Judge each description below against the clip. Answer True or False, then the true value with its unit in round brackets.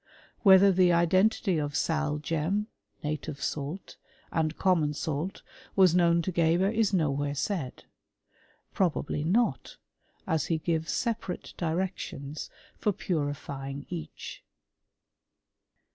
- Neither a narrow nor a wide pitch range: True (4.0 semitones)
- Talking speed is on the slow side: True (110 wpm)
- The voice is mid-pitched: True (165 Hz)